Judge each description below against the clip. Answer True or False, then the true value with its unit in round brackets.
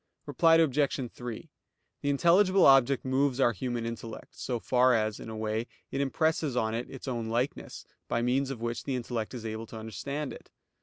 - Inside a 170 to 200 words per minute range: True (190 wpm)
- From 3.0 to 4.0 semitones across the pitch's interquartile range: True (3.4 semitones)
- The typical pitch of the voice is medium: False (125 Hz)